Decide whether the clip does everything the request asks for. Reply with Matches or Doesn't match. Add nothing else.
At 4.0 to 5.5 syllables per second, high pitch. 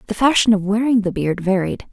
Doesn't match